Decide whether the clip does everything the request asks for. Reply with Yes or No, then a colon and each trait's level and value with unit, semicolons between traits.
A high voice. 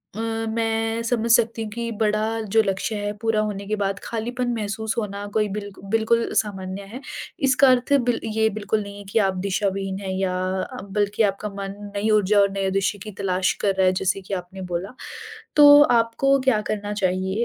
Yes: high, 210 Hz